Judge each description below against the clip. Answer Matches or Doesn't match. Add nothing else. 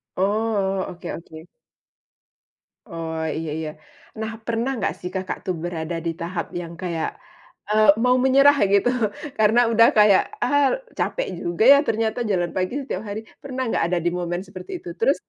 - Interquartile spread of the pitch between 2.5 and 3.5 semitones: Doesn't match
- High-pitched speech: Matches